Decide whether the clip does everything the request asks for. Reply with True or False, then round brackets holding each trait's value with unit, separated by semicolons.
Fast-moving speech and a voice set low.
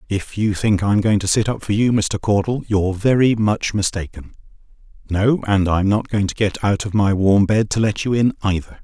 True (225 wpm; 100 Hz)